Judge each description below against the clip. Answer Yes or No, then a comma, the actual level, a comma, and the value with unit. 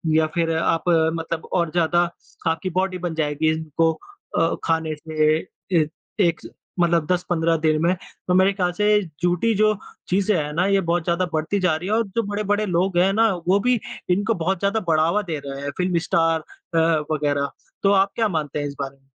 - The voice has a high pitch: No, medium, 170 Hz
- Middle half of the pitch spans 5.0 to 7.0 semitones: No, average, 3.1 semitones